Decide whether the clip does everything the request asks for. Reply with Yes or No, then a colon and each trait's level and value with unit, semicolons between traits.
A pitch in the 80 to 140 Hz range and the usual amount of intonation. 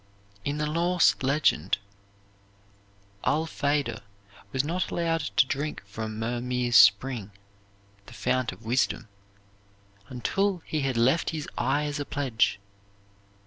Yes: low, 135 Hz; average, 4.3 semitones